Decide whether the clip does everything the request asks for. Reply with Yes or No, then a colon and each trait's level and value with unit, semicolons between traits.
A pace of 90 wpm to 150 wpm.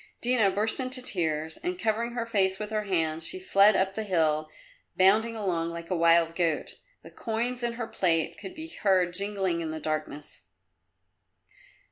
No: average, 170 wpm